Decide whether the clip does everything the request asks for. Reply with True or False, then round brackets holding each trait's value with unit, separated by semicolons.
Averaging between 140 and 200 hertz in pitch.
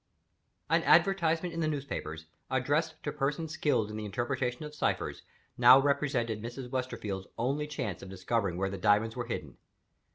False (130 Hz)